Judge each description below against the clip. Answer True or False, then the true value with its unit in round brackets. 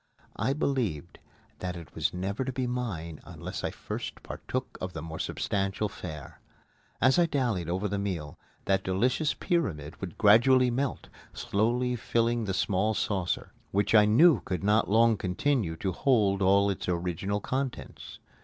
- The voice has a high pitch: False (100 Hz)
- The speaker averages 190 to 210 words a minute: False (160 wpm)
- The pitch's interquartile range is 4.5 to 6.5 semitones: True (5.1 semitones)